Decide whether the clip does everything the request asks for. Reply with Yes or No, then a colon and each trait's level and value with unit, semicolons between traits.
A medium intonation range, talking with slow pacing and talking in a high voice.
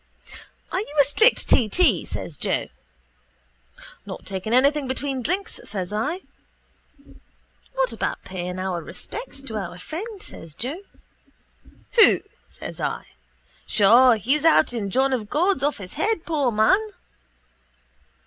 No: wide, 8.2 semitones; slow, 130 wpm; very high, 260 Hz